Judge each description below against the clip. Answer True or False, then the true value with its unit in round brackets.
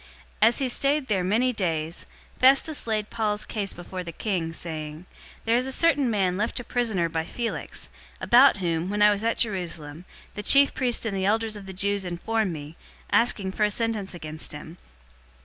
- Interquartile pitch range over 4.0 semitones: True (4.8 semitones)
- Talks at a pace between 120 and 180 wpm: False (195 wpm)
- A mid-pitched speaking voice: False (205 Hz)